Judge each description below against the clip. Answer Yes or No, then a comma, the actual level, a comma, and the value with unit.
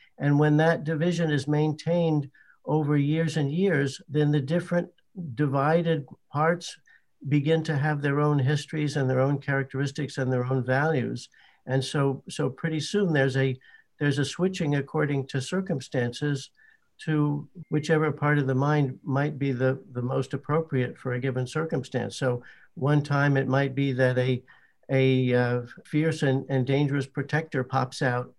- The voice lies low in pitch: No, medium, 145 Hz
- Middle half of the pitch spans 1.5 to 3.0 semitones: Yes, narrow, 2.5 semitones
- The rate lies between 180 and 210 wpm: No, average, 160 wpm